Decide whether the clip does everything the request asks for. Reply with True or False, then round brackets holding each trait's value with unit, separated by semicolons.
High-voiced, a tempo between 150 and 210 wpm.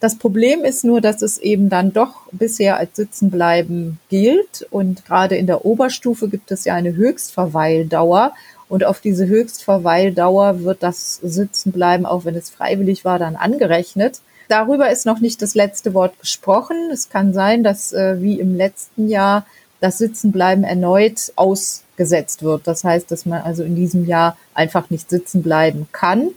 True (195 Hz; 160 wpm)